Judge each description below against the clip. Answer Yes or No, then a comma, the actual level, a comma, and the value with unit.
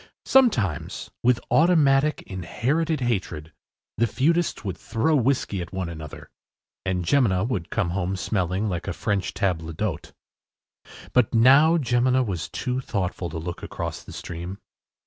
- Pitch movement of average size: No, wide, 6.6 semitones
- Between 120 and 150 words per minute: Yes, average, 140 wpm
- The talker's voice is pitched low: Yes, low, 105 Hz